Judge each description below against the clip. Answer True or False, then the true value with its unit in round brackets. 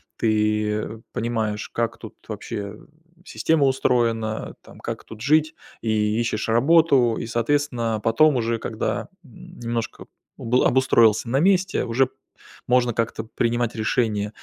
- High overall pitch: False (115 Hz)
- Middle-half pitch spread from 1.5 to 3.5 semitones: True (2.6 semitones)